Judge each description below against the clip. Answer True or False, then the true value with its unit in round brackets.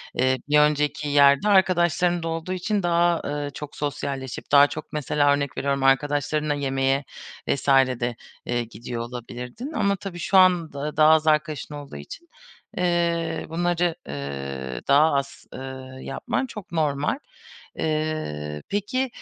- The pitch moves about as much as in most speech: True (4.2 semitones)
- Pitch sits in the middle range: True (150 Hz)